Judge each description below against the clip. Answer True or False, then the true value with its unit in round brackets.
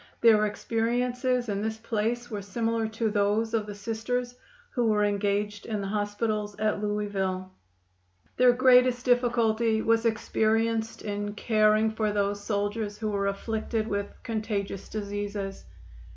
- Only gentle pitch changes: True (1.8 semitones)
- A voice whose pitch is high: True (215 Hz)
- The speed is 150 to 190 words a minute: False (135 wpm)